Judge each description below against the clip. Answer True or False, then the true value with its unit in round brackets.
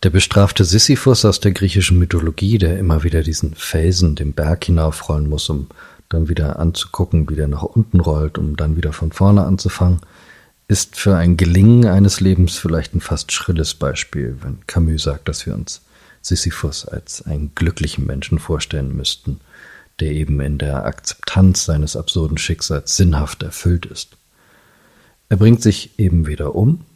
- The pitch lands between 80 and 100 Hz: True (85 Hz)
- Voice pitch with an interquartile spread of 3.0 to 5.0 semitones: True (3.6 semitones)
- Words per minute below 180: True (160 wpm)